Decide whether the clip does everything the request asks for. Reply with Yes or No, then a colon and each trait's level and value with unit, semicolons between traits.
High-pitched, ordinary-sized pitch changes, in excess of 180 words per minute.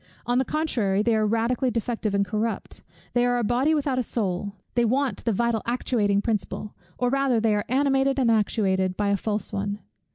Yes: high, 230 Hz; average, 3.3 semitones; average, 195 wpm